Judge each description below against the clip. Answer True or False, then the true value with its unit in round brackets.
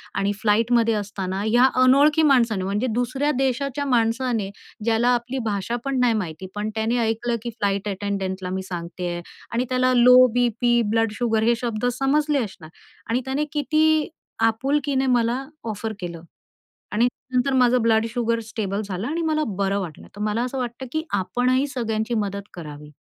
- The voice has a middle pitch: False (230 Hz)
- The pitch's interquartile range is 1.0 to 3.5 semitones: False (4.0 semitones)